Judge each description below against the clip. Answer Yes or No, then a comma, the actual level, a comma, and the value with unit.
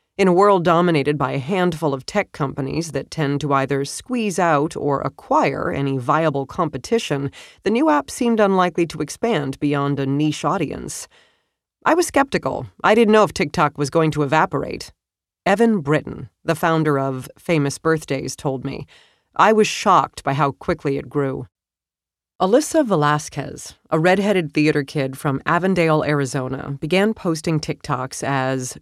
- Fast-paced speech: No, average, 155 wpm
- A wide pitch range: No, average, 4.7 semitones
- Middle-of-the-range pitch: Yes, medium, 150 Hz